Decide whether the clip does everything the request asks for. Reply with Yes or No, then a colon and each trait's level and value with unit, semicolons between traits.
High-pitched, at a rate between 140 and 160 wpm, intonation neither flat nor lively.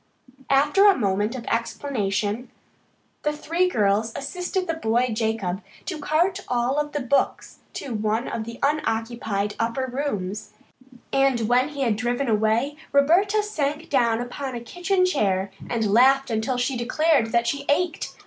Yes: very high, 250 Hz; average, 150 wpm; average, 4.8 semitones